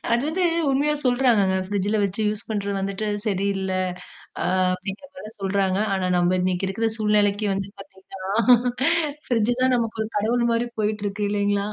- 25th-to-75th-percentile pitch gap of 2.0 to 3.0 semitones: Yes, narrow, 2.6 semitones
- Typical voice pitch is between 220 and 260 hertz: No, high, 205 Hz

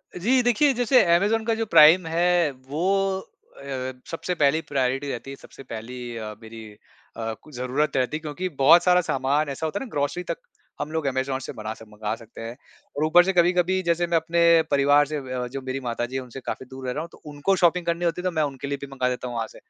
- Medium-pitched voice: Yes, medium, 145 Hz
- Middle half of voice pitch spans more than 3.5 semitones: Yes, average, 5.1 semitones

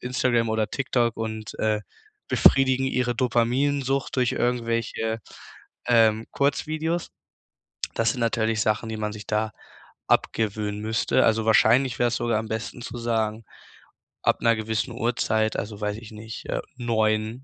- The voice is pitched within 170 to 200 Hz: No, low, 115 Hz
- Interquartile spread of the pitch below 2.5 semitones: Yes, narrow, 2.0 semitones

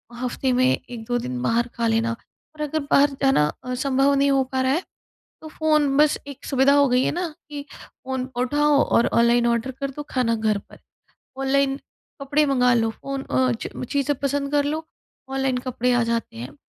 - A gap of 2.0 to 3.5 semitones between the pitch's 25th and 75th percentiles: Yes, average, 2.9 semitones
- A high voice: Yes, very high, 265 Hz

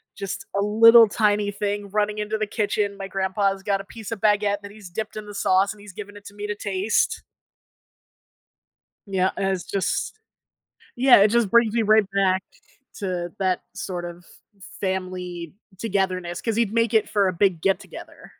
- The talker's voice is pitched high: Yes, high, 200 Hz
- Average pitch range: No, narrow, 2.0 semitones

